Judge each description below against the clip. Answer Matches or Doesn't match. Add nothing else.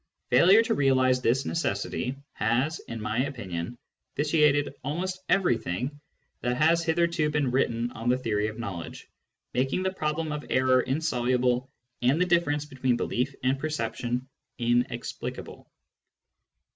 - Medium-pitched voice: Doesn't match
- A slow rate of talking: Matches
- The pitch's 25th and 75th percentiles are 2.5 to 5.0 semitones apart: Matches